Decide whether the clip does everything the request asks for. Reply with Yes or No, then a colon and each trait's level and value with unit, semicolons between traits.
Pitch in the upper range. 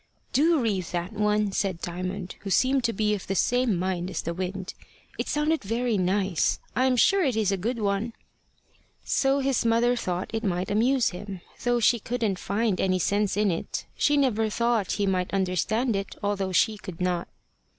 Yes: high, 205 Hz